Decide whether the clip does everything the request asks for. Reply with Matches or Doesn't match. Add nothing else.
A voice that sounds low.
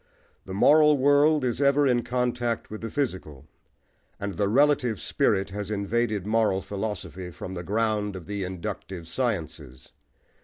Matches